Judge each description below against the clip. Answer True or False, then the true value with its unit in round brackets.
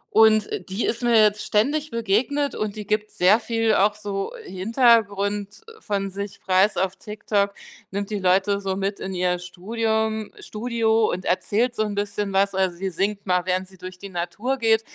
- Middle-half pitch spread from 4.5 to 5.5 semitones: False (2.4 semitones)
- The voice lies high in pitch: True (205 Hz)